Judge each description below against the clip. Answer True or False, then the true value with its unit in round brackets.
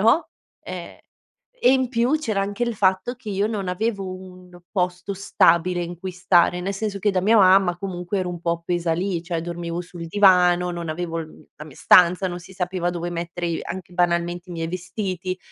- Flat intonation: True (2.2 semitones)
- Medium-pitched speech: True (180 Hz)